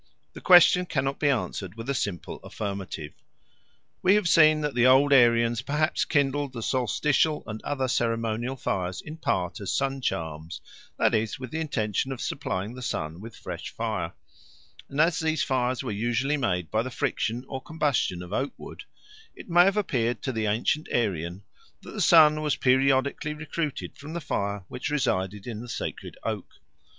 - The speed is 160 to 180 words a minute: Yes, average, 175 wpm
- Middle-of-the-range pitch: No, low, 130 Hz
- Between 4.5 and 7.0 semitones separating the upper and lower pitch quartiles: Yes, wide, 5.5 semitones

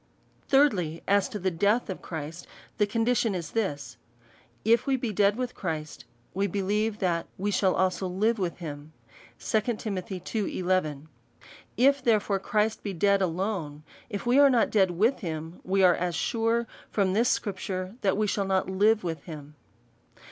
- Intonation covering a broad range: No, average, 3.8 semitones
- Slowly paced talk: No, average, 160 wpm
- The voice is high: Yes, high, 195 Hz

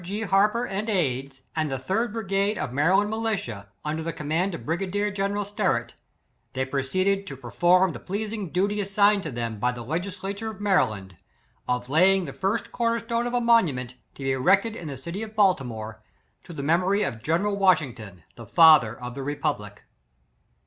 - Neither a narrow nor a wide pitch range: No, wide, 7.3 semitones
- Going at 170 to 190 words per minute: Yes, average, 185 wpm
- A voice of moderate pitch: Yes, medium, 180 Hz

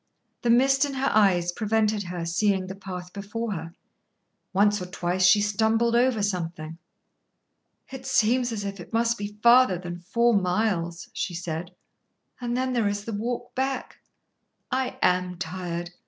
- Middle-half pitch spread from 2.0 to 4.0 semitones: No, average, 4.6 semitones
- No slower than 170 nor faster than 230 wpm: No, average, 155 wpm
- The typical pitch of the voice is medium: No, high, 205 Hz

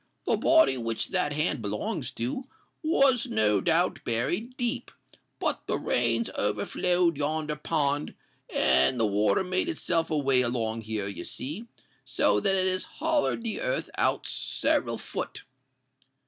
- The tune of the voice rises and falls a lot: Yes, wide, 8.5 semitones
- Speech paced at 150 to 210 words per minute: No, average, 140 wpm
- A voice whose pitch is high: No, medium, 145 Hz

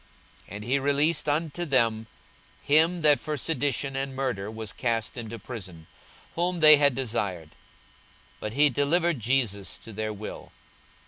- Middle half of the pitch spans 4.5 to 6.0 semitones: Yes, average, 5.2 semitones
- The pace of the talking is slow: No, average, 145 wpm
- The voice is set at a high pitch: No, low, 130 Hz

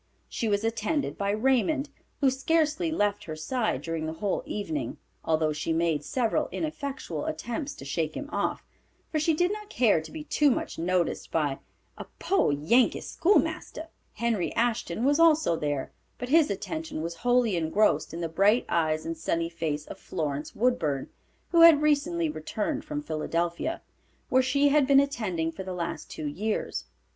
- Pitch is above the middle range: Yes, high, 215 Hz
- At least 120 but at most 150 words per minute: No, average, 170 wpm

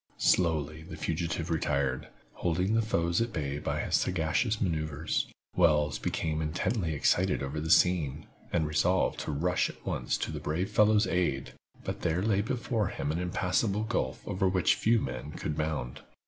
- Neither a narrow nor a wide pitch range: Yes, average, 3.5 semitones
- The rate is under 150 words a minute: No, average, 165 wpm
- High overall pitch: No, very low, 85 Hz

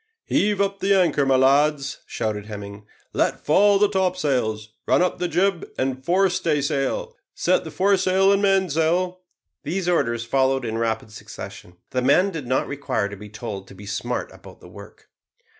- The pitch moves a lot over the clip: Yes, wide, 8.3 semitones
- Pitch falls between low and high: Yes, medium, 145 Hz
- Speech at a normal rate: Yes, average, 170 wpm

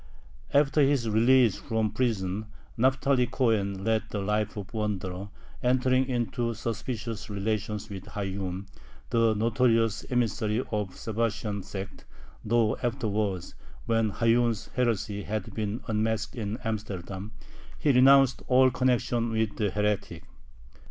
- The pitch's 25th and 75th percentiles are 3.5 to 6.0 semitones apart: No, narrow, 2.6 semitones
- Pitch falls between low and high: No, low, 110 Hz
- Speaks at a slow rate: Yes, slow, 125 wpm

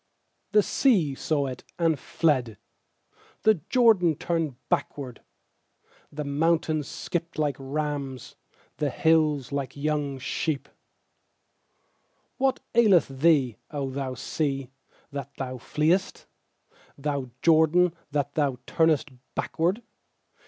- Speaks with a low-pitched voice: No, medium, 150 Hz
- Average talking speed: No, slow, 105 wpm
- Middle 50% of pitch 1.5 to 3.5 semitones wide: Yes, average, 3.2 semitones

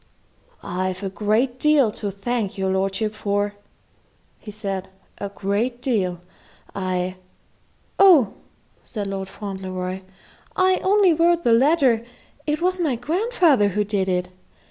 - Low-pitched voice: No, high, 210 Hz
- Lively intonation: Yes, wide, 6.6 semitones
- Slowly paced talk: Yes, slow, 125 wpm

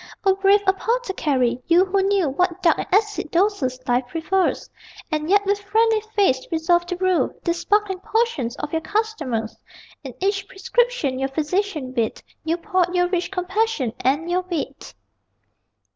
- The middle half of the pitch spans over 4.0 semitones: Yes, average, 4.9 semitones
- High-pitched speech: Yes, very high, 360 Hz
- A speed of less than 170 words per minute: Yes, average, 155 wpm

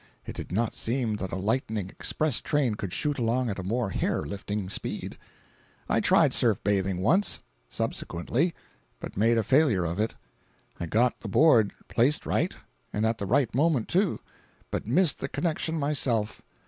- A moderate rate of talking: Yes, average, 170 wpm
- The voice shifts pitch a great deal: Yes, wide, 5.7 semitones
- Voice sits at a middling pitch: No, low, 115 Hz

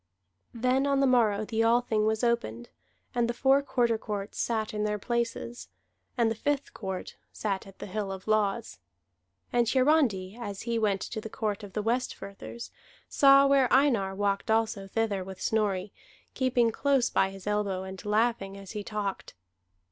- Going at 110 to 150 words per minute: No, average, 170 wpm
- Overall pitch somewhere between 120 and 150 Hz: No, high, 220 Hz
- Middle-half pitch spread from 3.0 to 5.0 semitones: Yes, average, 3.3 semitones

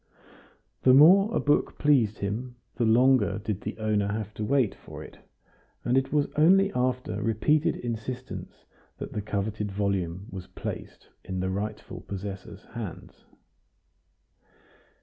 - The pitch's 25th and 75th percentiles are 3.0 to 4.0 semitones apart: No, average, 4.4 semitones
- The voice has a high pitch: No, low, 110 Hz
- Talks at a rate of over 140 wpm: No, slow, 135 wpm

